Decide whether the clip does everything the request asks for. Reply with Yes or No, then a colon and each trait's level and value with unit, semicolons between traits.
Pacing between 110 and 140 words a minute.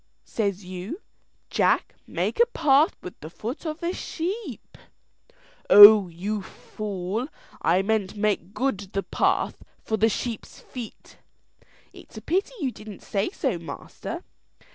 Yes: slow, 135 wpm